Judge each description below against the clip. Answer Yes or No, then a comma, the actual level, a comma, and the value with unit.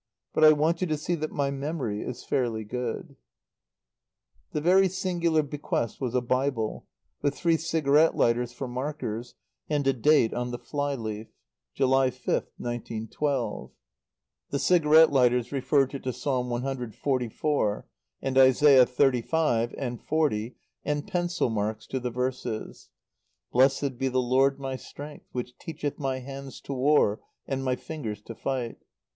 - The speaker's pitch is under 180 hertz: Yes, low, 135 Hz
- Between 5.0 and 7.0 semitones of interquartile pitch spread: No, average, 3.4 semitones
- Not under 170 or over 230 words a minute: No, average, 145 wpm